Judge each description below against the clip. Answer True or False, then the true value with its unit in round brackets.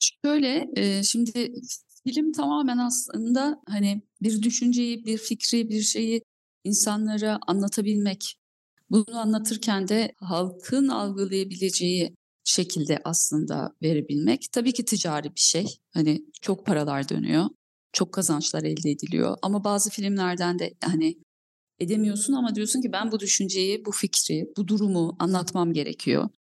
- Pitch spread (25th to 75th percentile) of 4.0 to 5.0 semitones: True (4.5 semitones)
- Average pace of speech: True (120 wpm)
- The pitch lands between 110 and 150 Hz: False (205 Hz)